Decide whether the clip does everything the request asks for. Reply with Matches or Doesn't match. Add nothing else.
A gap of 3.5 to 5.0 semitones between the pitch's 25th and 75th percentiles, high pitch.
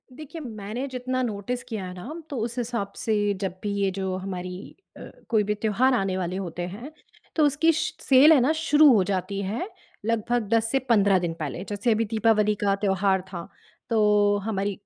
Matches